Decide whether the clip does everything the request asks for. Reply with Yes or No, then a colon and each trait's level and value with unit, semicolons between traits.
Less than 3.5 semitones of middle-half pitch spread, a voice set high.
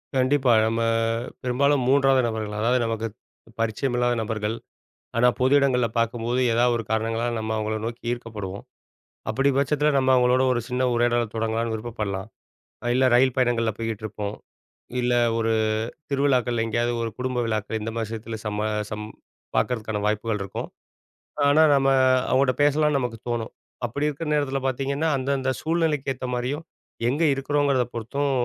No: average, 3.1 semitones; low, 120 Hz